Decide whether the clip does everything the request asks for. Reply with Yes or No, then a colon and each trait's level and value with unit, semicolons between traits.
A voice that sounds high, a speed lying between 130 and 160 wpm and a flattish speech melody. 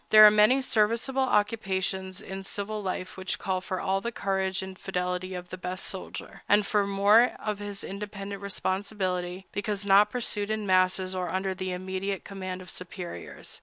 No: high, 195 Hz; average, 170 wpm; narrow, 1.9 semitones